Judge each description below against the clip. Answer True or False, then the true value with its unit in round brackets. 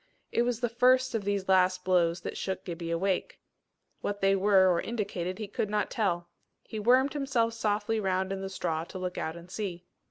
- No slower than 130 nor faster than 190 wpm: False (200 wpm)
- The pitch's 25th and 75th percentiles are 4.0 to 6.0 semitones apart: False (3.5 semitones)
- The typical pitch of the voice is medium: False (195 Hz)